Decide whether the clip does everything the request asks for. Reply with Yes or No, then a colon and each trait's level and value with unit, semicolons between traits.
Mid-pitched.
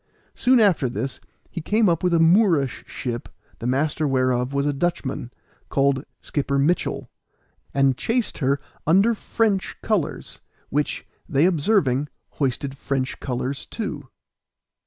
Yes: medium, 145 Hz